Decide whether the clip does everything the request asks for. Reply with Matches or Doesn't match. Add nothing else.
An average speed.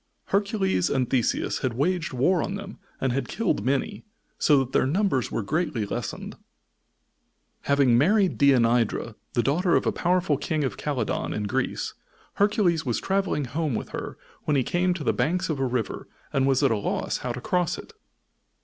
Matches